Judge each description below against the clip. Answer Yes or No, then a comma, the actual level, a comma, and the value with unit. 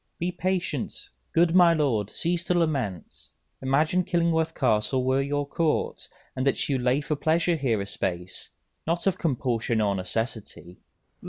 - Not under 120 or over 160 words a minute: Yes, average, 155 wpm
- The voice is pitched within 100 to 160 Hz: Yes, medium, 140 Hz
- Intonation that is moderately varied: No, wide, 6.3 semitones